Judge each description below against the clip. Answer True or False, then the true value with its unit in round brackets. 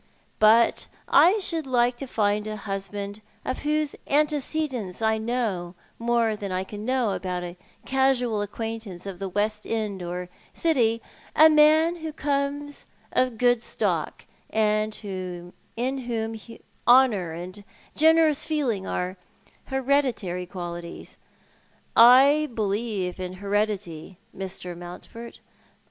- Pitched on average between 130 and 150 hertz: False (220 Hz)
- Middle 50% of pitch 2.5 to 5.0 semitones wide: False (5.6 semitones)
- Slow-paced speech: True (120 wpm)